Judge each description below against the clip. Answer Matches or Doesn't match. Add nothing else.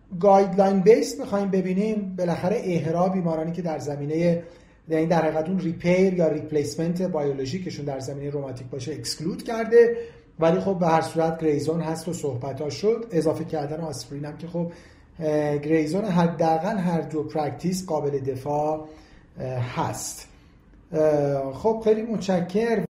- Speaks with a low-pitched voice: Doesn't match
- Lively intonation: Doesn't match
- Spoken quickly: Doesn't match